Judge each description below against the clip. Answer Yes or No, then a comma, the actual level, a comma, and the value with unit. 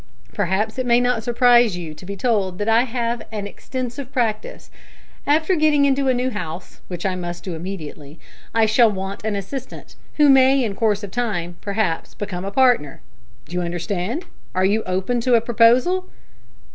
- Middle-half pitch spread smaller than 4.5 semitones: No, average, 4.9 semitones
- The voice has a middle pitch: No, high, 220 Hz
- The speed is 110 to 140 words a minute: No, average, 175 wpm